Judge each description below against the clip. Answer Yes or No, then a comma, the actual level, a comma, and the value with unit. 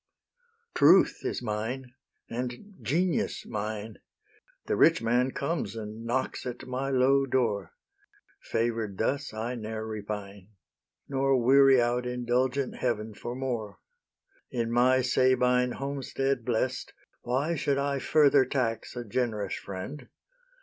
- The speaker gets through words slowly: Yes, slow, 120 wpm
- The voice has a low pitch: Yes, low, 125 Hz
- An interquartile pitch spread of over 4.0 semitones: No, average, 3.1 semitones